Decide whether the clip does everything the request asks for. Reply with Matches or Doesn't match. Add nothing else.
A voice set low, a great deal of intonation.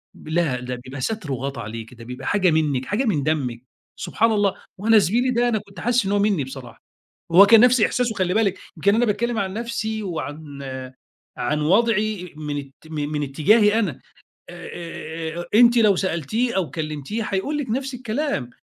Doesn't match